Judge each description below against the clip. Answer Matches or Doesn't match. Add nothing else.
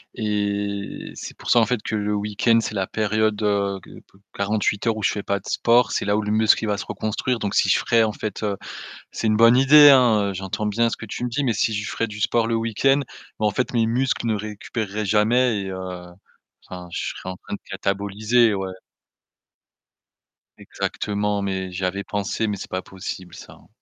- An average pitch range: Doesn't match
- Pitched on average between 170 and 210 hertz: Doesn't match